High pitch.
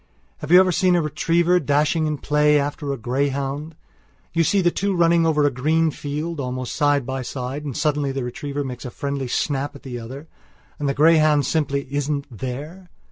No: medium, 145 Hz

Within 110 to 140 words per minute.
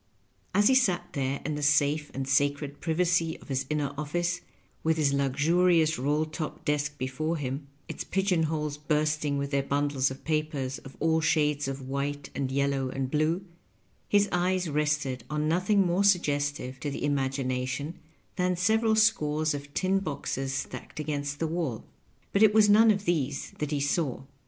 No: average, 165 wpm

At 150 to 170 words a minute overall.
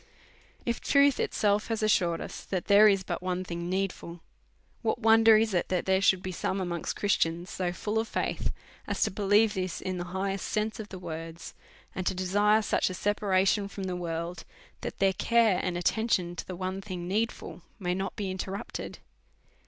No: average, 190 wpm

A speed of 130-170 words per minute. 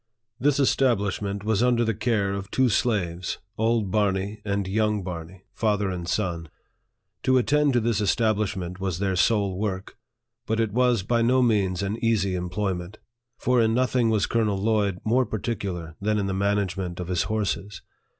Yes: average, 165 wpm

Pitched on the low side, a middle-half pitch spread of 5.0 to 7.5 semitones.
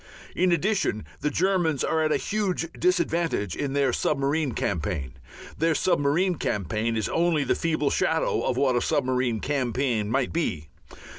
No: medium, 145 Hz; wide, 5.5 semitones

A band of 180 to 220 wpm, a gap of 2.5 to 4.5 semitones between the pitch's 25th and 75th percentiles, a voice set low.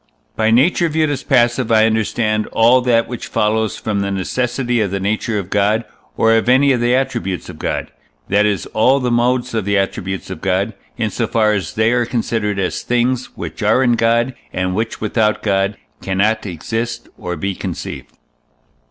Yes: average, 185 wpm; average, 3.2 semitones; low, 110 Hz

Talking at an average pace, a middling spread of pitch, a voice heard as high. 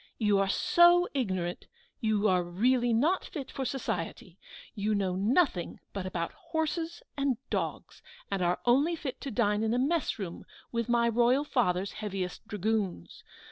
No: average, 155 wpm; wide, 5.7 semitones; high, 225 Hz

